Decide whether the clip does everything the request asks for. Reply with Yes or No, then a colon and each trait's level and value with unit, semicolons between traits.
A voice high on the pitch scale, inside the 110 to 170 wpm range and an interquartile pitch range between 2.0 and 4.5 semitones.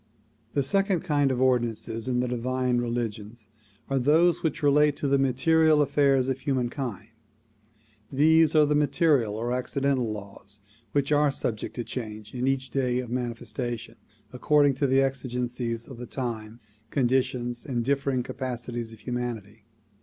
No: low, 125 Hz; average, 145 wpm; average, 2.7 semitones